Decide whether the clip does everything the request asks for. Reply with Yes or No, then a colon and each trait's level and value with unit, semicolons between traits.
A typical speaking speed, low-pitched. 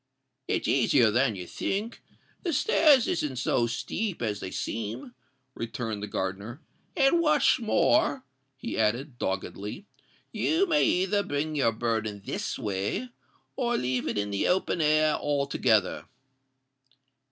No: slow, 130 wpm; low, 130 Hz